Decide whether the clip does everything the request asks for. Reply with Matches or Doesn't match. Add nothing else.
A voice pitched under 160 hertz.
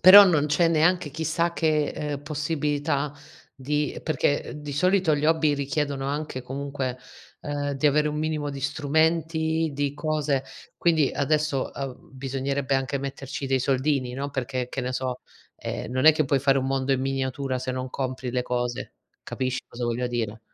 Matches